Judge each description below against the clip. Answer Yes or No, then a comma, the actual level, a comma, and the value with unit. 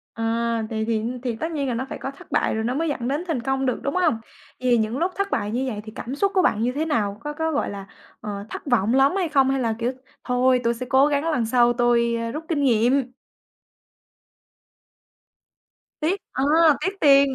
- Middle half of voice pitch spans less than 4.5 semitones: Yes, average, 3.9 semitones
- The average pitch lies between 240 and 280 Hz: Yes, very high, 255 Hz